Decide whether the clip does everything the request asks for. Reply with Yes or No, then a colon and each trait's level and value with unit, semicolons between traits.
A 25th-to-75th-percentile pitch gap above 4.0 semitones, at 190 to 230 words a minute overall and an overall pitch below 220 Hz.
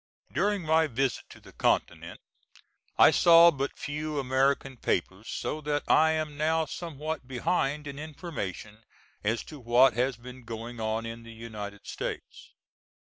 No: average, 5.0 semitones; average, 145 wpm; low, 135 Hz